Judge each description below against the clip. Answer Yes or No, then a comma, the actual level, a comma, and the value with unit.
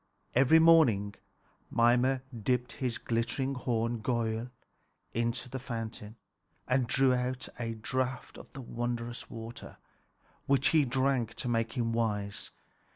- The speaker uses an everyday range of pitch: No, narrow, 2.2 semitones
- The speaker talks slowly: Yes, slow, 125 wpm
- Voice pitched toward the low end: Yes, low, 120 Hz